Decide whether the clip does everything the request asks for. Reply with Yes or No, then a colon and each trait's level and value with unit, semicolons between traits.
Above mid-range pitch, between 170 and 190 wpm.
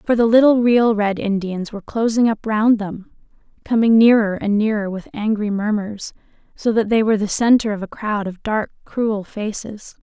Yes: high, 215 Hz; average, 185 wpm